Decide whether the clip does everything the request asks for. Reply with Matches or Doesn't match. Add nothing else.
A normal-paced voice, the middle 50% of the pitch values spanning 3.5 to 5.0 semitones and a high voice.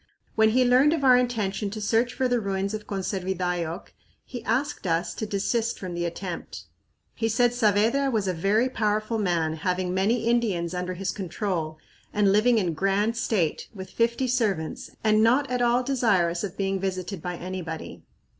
Matches